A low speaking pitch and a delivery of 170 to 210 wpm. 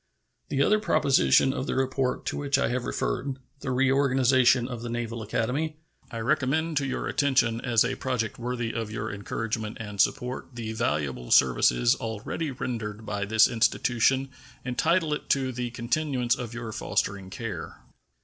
No: low, 120 Hz; average, 160 wpm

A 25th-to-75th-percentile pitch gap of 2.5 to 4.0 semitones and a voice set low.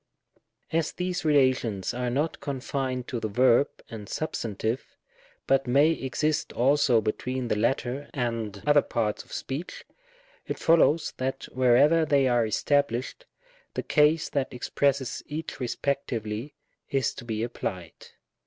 Yes: average, 3.6 semitones; low, 130 Hz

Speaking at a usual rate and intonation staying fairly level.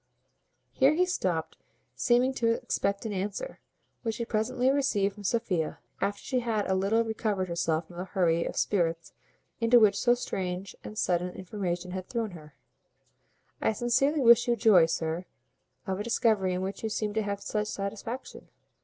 No: average, 170 wpm; average, 4.1 semitones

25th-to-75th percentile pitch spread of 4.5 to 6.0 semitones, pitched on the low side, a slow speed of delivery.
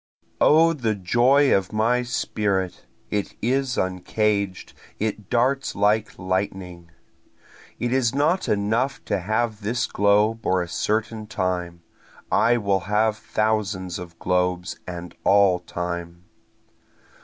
No: average, 3.8 semitones; low, 105 Hz; slow, 120 wpm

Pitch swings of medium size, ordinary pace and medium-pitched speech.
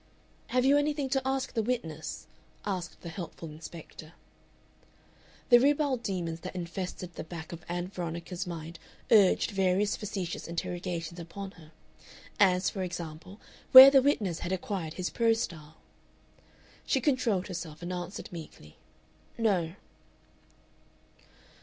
No: average, 4.7 semitones; slow, 130 wpm; medium, 180 Hz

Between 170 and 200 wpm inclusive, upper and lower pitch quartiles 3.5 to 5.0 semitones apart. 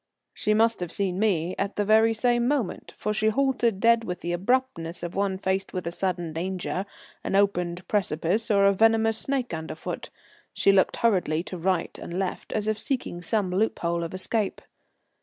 Yes: average, 185 wpm; average, 3.9 semitones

